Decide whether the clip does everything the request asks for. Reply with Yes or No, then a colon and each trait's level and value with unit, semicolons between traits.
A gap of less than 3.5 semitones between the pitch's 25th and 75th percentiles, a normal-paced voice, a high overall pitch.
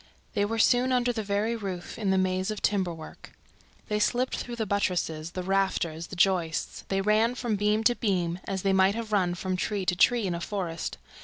No: average, 3.1 semitones; fast, 215 wpm; high, 195 Hz